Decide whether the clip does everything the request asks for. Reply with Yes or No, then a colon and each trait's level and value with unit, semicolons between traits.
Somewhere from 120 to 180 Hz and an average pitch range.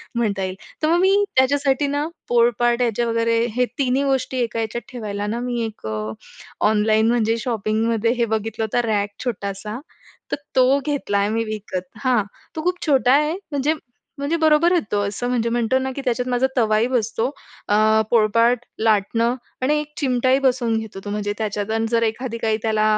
No: high, 230 Hz; average, 3.1 semitones